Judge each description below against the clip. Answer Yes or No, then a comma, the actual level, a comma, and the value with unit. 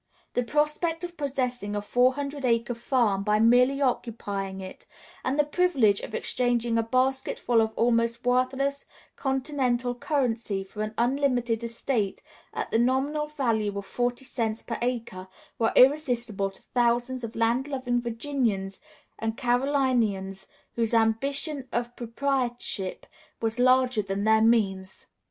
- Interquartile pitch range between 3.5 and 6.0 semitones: No, average, 3.0 semitones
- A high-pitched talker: Yes, high, 240 Hz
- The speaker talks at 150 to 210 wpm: No, slow, 135 wpm